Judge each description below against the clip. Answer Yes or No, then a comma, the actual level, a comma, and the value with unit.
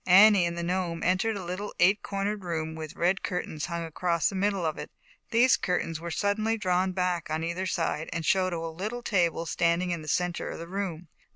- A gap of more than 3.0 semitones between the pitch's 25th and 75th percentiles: No, average, 2.7 semitones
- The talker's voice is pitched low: No, medium, 180 Hz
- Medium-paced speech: No, fast, 215 wpm